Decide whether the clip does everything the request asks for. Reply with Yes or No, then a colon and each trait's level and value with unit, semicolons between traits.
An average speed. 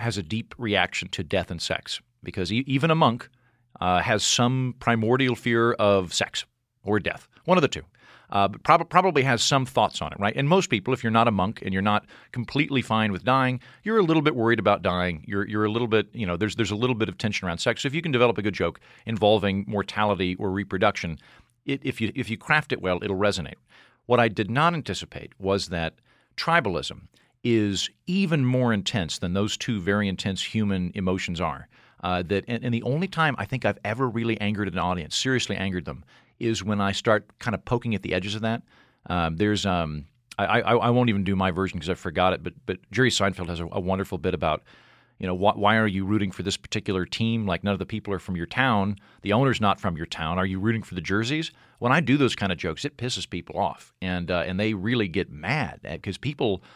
No: fast, 235 wpm